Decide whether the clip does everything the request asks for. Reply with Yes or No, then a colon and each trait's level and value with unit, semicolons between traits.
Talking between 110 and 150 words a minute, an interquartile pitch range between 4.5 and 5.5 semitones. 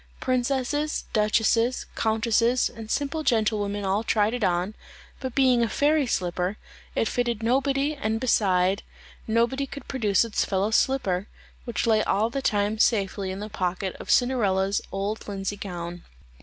No: average, 145 wpm; average, 3.9 semitones